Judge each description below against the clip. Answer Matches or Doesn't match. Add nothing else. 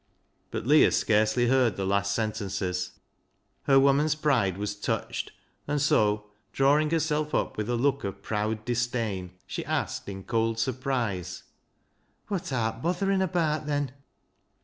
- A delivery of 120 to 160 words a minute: Matches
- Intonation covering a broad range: Matches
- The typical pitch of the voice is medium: Doesn't match